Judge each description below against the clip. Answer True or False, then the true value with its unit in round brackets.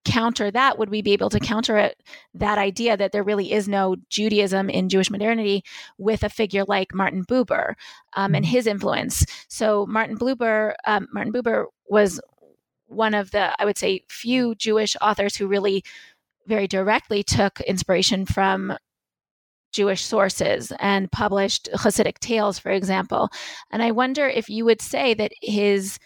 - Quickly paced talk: False (160 wpm)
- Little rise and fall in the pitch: True (2.3 semitones)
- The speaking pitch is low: False (210 Hz)